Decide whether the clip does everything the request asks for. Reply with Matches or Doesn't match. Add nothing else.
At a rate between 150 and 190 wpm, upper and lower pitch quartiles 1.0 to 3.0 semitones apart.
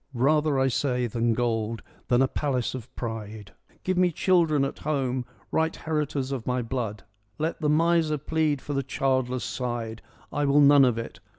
Doesn't match